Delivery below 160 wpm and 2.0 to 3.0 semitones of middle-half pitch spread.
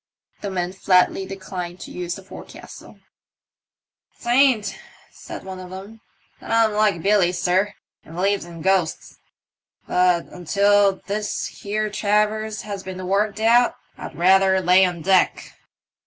Yes: slow, 135 wpm; narrow, 2.5 semitones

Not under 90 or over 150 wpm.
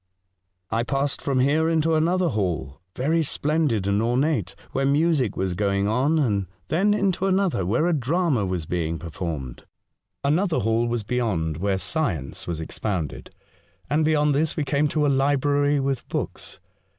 No: average, 165 wpm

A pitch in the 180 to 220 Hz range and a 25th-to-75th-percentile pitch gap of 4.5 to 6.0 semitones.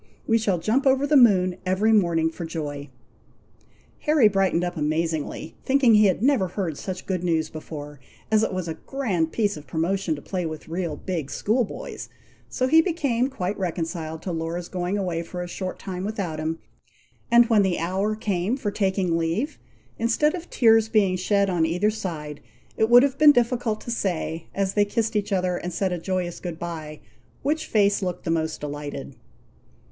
Yes: medium, 185 Hz; average, 5.0 semitones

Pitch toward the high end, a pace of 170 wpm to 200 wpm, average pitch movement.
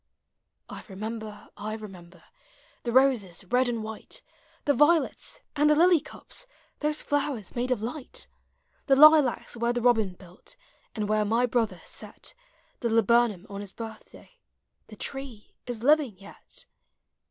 No: high, 235 Hz; average, 150 wpm; average, 4.6 semitones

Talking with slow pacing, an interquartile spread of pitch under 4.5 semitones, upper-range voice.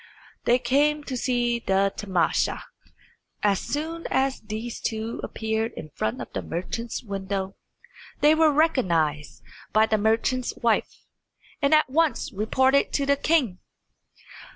No: slow, 130 wpm; wide, 5.5 semitones; high, 235 Hz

